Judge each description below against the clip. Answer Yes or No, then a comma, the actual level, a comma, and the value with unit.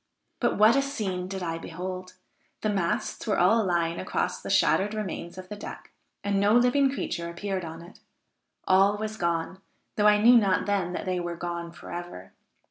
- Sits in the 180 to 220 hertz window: Yes, high, 190 Hz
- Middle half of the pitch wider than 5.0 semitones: No, average, 3.3 semitones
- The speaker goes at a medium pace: Yes, average, 185 wpm